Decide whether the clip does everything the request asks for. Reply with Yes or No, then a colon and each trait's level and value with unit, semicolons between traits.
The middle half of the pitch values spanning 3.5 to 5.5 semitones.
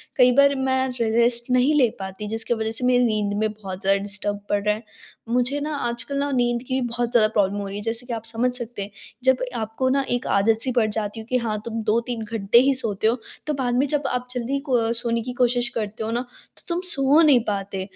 No: average, 2.7 semitones